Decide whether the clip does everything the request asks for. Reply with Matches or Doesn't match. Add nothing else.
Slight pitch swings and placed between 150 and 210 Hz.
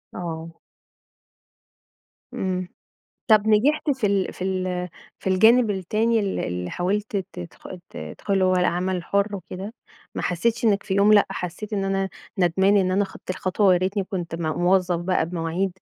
Matches